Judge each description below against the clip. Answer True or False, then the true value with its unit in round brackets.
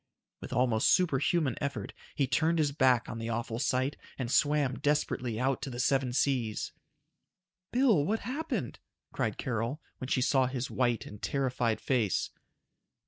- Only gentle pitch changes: False (3.1 semitones)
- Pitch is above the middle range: False (130 Hz)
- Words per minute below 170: True (150 wpm)